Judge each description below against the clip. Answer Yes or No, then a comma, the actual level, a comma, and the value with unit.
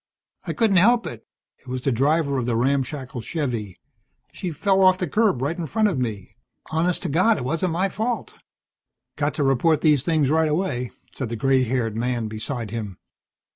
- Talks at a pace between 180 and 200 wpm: Yes, average, 190 wpm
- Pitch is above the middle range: No, medium, 140 Hz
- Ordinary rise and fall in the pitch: No, wide, 5.9 semitones